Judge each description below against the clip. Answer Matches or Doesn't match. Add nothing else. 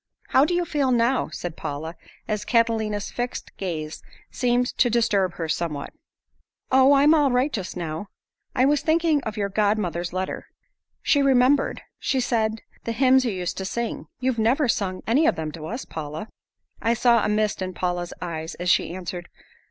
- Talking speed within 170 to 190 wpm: Matches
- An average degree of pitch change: Doesn't match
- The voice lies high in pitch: Matches